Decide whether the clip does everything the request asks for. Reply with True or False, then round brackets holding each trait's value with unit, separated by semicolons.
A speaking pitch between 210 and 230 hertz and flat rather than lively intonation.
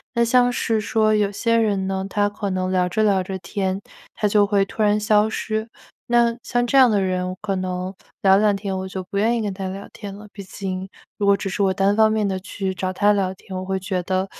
False (200 Hz; 2.1 semitones)